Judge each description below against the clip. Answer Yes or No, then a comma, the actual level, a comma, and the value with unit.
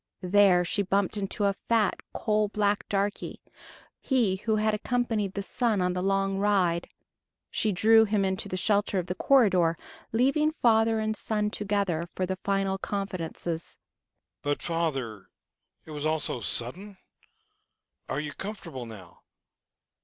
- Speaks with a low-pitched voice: No, high, 195 Hz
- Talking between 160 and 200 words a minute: No, average, 145 wpm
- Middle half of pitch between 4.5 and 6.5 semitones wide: No, average, 3.3 semitones